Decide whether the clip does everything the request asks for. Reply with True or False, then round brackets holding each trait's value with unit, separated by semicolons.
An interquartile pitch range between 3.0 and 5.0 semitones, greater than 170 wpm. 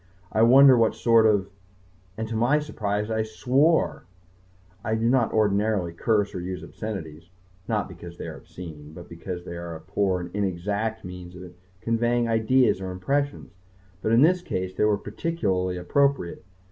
False (4.2 semitones; 165 wpm)